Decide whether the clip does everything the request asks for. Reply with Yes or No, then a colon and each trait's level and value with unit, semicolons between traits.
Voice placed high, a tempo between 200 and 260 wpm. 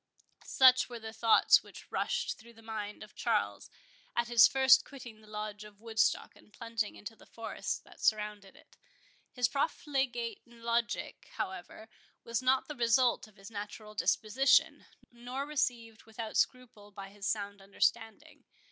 No: high, 225 Hz; average, 150 wpm